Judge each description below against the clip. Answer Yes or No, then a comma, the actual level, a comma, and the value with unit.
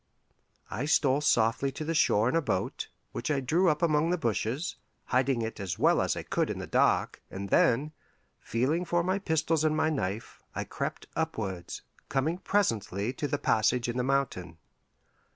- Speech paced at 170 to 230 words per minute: Yes, average, 180 wpm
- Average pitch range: No, wide, 5.8 semitones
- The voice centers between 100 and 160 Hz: Yes, low, 135 Hz